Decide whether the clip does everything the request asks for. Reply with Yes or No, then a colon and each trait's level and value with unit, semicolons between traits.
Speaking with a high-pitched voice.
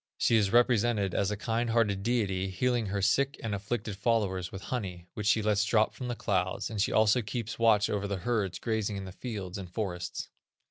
No: low, 105 Hz